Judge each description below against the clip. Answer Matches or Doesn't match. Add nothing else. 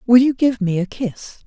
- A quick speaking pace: Matches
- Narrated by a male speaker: Doesn't match